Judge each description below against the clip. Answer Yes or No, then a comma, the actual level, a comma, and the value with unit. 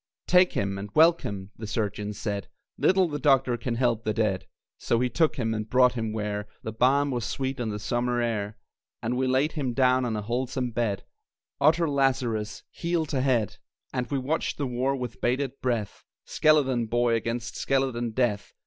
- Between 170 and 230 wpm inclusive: Yes, average, 185 wpm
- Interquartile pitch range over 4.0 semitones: No, average, 3.5 semitones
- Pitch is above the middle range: No, low, 120 Hz